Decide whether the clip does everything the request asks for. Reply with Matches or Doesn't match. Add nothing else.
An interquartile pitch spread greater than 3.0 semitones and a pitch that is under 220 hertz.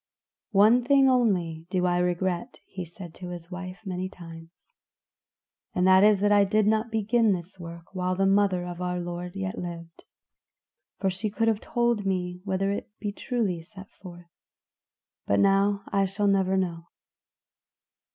Doesn't match